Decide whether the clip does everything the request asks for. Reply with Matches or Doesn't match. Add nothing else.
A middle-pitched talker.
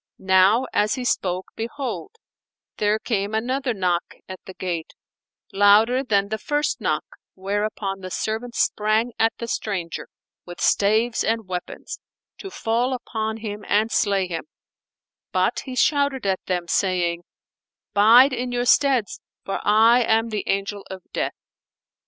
Doesn't match